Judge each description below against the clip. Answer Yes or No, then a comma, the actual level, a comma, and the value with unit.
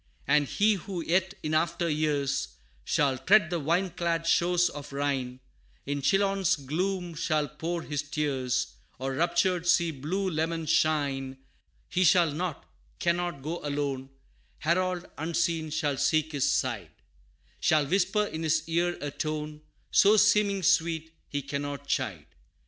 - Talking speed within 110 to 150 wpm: Yes, average, 140 wpm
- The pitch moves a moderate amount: Yes, average, 3.5 semitones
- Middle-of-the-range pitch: Yes, medium, 160 Hz